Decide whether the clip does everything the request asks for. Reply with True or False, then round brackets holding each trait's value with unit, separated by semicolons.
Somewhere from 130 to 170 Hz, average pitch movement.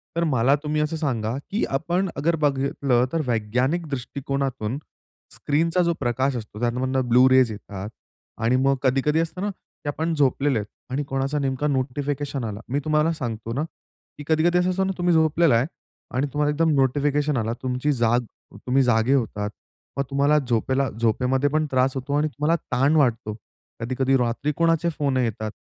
True (135 Hz; 3.4 semitones)